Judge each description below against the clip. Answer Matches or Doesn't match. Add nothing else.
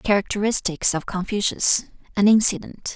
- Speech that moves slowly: Matches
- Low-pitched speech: Doesn't match